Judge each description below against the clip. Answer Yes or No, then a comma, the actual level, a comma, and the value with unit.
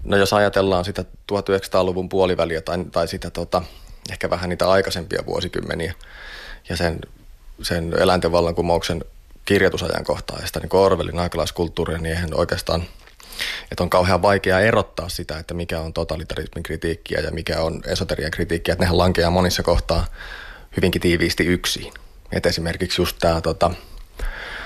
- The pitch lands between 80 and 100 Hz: Yes, very low, 85 Hz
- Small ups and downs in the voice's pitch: Yes, narrow, 1.8 semitones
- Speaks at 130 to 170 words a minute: Yes, average, 135 wpm